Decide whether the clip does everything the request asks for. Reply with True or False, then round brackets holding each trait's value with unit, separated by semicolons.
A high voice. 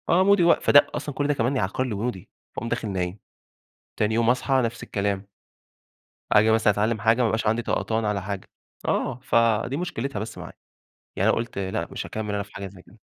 False (110 Hz)